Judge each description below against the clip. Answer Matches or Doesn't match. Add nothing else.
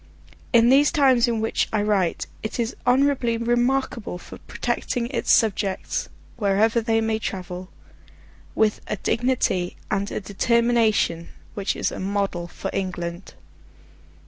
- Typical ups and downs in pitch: Matches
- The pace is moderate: Doesn't match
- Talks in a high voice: Matches